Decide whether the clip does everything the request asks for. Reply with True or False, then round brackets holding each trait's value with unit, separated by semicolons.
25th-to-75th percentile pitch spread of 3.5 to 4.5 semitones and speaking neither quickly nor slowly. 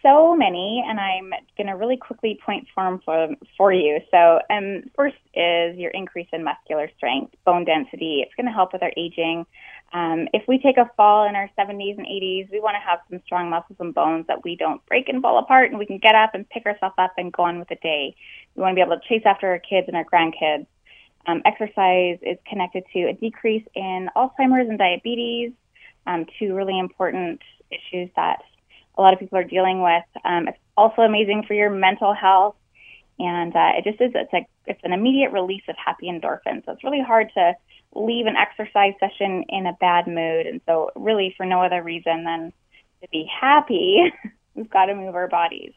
False (4.0 semitones; 210 wpm)